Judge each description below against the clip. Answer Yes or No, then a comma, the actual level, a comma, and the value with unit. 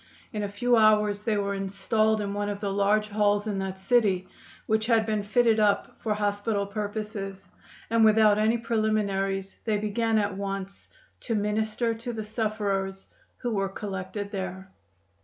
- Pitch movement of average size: No, narrow, 1.6 semitones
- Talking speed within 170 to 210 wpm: No, average, 160 wpm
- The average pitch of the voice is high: Yes, high, 210 Hz